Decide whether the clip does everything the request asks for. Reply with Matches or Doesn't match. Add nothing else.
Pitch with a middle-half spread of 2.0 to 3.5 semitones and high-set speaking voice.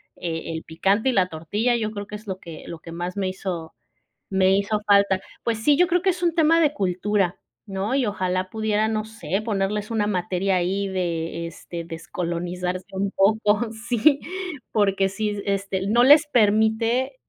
Matches